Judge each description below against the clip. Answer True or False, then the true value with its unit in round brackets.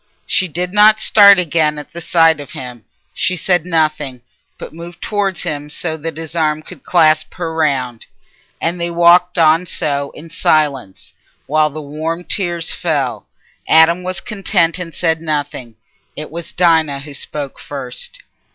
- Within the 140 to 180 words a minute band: True (160 wpm)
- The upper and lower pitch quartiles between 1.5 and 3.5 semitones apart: True (2.7 semitones)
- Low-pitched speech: False (160 Hz)